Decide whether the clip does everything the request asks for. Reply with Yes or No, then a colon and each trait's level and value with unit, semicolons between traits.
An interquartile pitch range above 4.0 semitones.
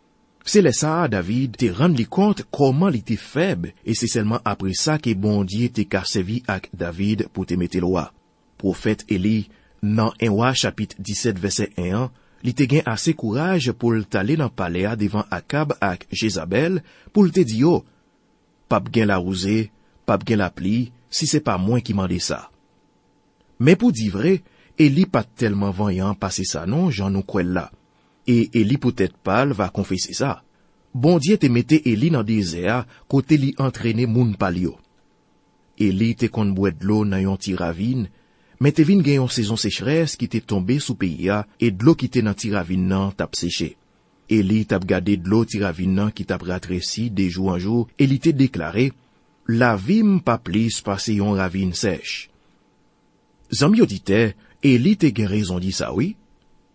Yes: average, 4.6 semitones